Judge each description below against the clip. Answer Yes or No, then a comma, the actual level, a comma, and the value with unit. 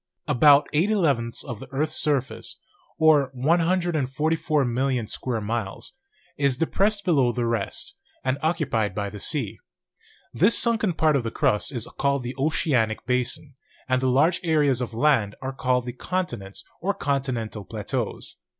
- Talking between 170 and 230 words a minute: No, average, 150 wpm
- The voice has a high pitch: No, low, 135 Hz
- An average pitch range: Yes, average, 4.7 semitones